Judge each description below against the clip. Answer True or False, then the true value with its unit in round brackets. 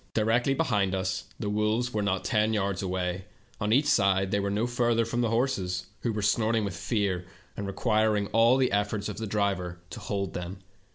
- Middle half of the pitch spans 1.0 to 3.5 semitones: True (2.8 semitones)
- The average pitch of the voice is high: False (105 Hz)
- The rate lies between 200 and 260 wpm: True (205 wpm)